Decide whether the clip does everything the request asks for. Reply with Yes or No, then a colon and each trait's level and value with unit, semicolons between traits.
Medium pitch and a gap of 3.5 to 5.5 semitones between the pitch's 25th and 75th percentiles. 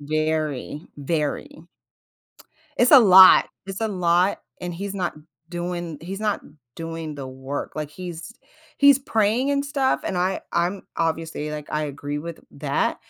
Yes: medium, 170 Hz; average, 4.2 semitones